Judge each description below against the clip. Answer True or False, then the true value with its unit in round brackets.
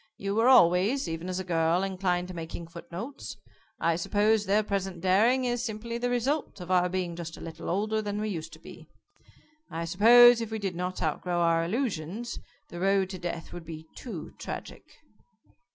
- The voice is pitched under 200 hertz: True (185 Hz)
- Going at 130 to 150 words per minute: False (185 wpm)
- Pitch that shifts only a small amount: False (4.3 semitones)